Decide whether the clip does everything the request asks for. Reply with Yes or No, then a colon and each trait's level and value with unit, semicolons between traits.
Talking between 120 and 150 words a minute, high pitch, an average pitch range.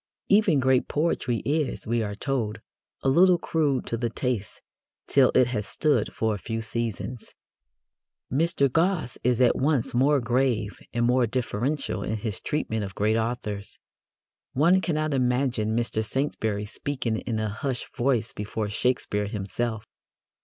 No: average, 145 wpm; low, 120 Hz; average, 3.9 semitones